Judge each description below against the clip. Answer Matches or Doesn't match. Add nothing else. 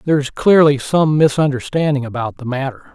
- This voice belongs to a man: Matches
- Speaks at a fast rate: Doesn't match